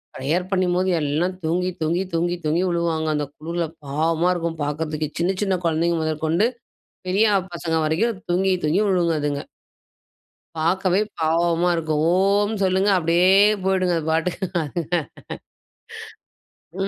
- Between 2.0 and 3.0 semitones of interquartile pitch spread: Yes, average, 2.7 semitones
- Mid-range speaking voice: Yes, medium, 170 Hz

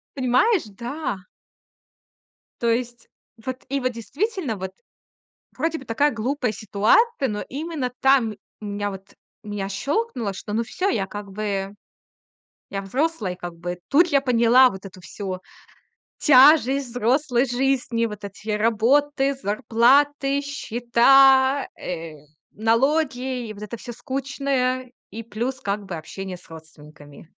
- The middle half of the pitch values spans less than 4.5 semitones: No, average, 4.9 semitones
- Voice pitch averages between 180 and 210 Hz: No, high, 240 Hz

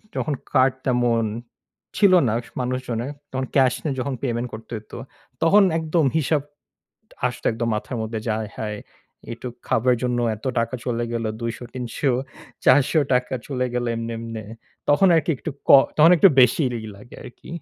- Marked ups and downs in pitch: No, average, 3.2 semitones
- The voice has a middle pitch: No, low, 125 Hz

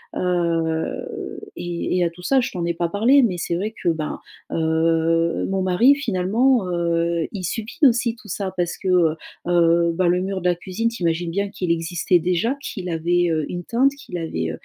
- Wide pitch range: No, average, 3.2 semitones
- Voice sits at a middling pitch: Yes, medium, 175 Hz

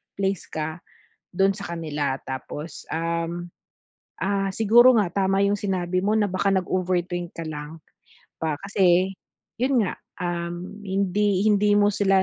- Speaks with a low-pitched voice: No, medium, 185 Hz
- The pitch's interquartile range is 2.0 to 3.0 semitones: Yes, average, 2.7 semitones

